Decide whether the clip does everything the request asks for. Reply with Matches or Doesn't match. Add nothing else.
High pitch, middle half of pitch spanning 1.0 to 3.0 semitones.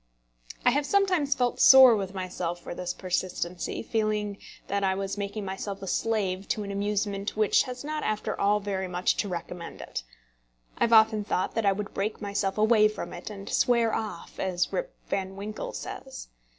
Matches